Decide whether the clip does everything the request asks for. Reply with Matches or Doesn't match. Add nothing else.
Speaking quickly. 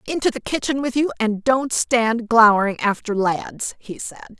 Doesn't match